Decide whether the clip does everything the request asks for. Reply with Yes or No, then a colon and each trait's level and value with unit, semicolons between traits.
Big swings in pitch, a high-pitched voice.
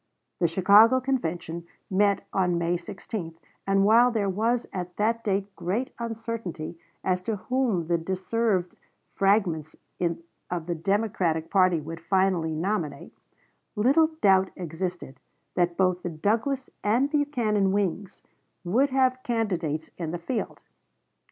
No: average, 4.6 semitones; high, 195 Hz